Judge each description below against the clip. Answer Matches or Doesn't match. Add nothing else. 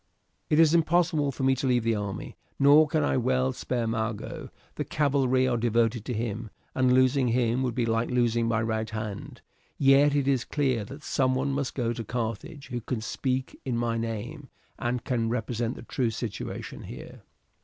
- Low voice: Matches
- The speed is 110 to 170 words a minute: Doesn't match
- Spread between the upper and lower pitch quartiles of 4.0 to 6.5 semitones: Doesn't match